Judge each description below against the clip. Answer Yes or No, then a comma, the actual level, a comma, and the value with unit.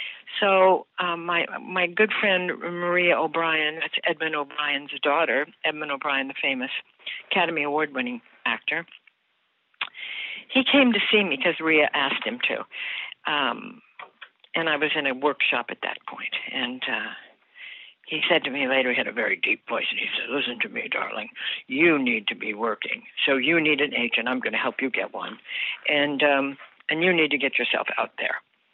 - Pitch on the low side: No, medium, 170 Hz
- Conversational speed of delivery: Yes, average, 180 wpm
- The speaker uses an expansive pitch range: Yes, wide, 8.6 semitones